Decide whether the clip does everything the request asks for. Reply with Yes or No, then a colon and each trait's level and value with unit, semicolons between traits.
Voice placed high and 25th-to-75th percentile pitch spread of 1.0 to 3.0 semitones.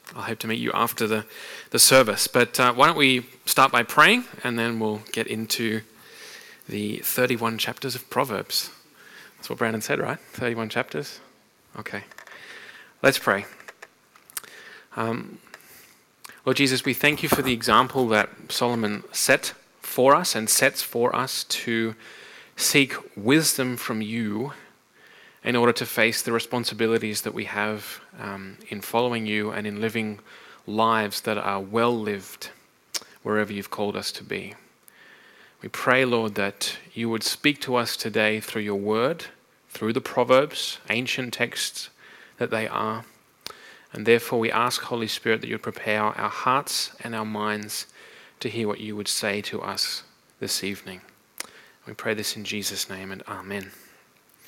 No: low, 115 Hz; narrow, 2.6 semitones